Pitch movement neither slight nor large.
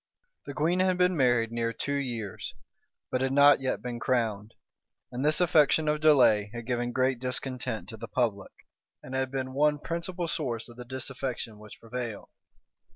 Yes: average, 3.5 semitones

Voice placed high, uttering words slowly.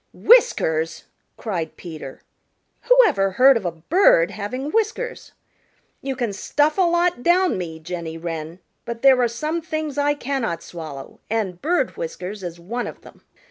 No: high, 235 Hz; average, 155 wpm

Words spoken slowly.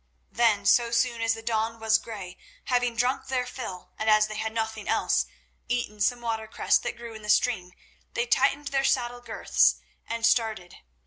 No: average, 180 wpm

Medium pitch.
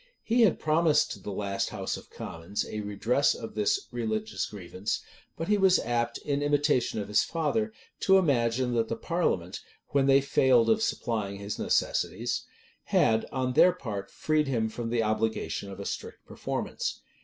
No: low, 120 Hz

